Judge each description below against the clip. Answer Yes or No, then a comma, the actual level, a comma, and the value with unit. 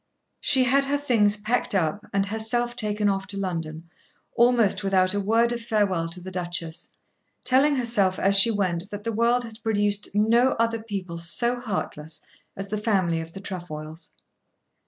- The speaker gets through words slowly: No, average, 170 wpm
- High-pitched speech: Yes, high, 205 Hz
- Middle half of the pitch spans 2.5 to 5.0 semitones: Yes, average, 3.9 semitones